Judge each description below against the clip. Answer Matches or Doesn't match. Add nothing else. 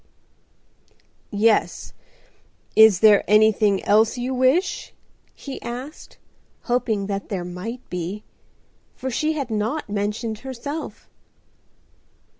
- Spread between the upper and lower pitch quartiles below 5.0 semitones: Matches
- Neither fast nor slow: Doesn't match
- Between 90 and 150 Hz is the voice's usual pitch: Doesn't match